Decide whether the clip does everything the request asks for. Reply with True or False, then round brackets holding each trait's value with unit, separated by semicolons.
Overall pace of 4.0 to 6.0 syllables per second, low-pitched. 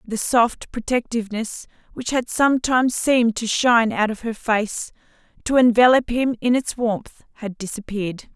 False (4.9 syllables/s; 230 Hz)